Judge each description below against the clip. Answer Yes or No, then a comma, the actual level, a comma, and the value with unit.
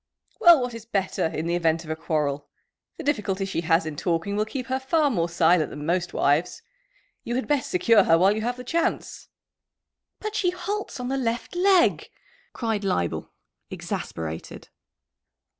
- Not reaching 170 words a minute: No, average, 175 wpm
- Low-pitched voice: No, high, 205 Hz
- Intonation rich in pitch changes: Yes, wide, 8.1 semitones